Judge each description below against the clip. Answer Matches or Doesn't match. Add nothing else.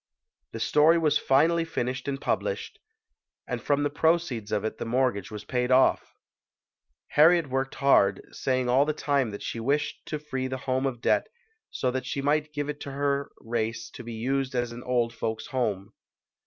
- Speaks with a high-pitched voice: Doesn't match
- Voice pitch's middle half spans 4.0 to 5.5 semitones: Doesn't match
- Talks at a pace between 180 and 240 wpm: Matches